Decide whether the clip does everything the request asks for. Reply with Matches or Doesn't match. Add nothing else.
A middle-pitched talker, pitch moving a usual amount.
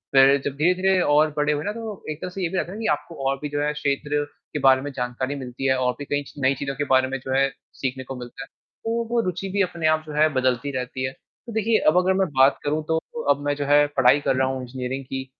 Matches